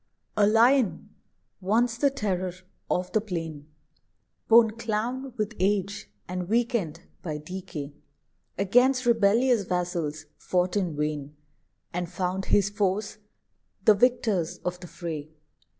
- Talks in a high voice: Yes, high, 195 Hz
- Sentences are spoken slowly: Yes, slow, 120 wpm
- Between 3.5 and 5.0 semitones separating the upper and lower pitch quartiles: Yes, average, 4.3 semitones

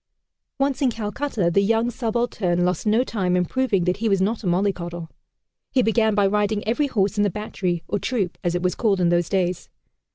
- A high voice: Yes, high, 205 Hz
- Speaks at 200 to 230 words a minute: Yes, fast, 205 wpm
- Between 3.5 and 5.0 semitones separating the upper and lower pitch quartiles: Yes, average, 4.0 semitones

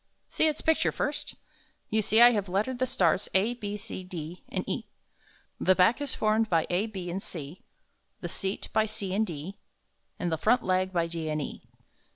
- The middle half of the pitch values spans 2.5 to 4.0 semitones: Yes, average, 3.7 semitones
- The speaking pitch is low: No, high, 190 Hz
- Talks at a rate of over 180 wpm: Yes, average, 195 wpm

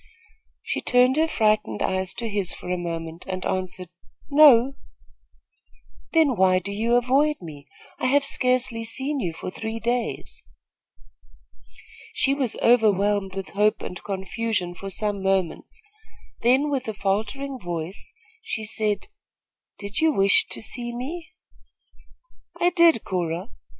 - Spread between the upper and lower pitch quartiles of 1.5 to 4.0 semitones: No, average, 5.2 semitones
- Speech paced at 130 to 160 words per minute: Yes, slow, 135 wpm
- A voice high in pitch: Yes, high, 215 Hz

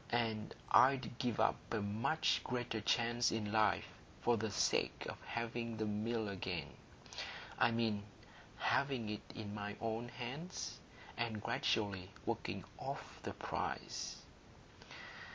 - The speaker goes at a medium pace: No, slow, 120 wpm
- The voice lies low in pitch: Yes, low, 115 Hz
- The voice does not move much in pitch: Yes, narrow, 2.2 semitones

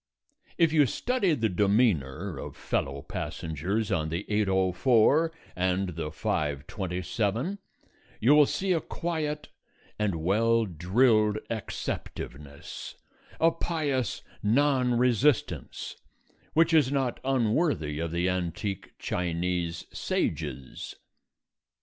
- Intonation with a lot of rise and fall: Yes, wide, 7.7 semitones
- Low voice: Yes, low, 105 Hz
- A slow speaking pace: Yes, slow, 100 wpm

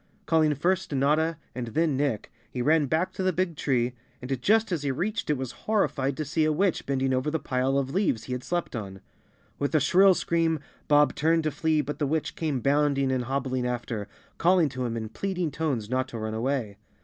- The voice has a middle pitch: Yes, medium, 145 Hz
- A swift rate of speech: Yes, fast, 215 wpm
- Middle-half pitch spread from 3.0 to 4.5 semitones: Yes, average, 4.0 semitones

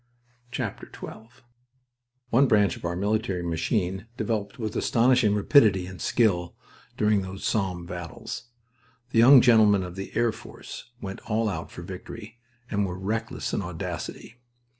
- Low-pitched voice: Yes, low, 105 Hz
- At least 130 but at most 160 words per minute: Yes, average, 140 wpm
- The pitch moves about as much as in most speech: Yes, average, 3.3 semitones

